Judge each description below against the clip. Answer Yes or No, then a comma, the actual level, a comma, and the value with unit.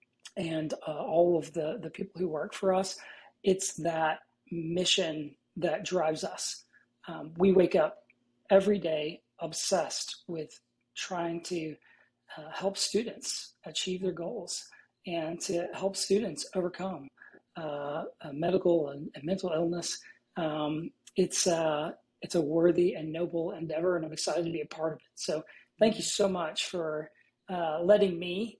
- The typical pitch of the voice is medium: Yes, medium, 170 Hz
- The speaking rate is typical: Yes, average, 145 wpm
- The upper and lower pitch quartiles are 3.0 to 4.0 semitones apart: Yes, average, 3.3 semitones